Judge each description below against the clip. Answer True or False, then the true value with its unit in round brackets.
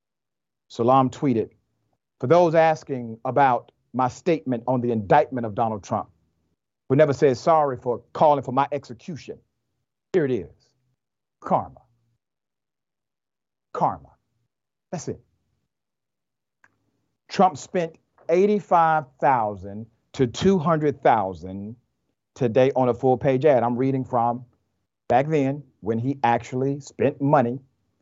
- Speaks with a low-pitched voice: True (130 Hz)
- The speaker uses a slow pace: True (110 wpm)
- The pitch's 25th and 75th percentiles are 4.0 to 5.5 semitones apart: False (3.5 semitones)